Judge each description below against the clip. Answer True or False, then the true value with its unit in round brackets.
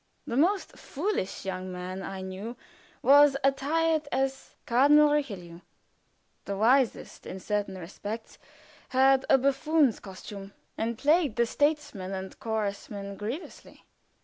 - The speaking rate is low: True (120 wpm)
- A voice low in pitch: False (235 Hz)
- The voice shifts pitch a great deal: True (6.6 semitones)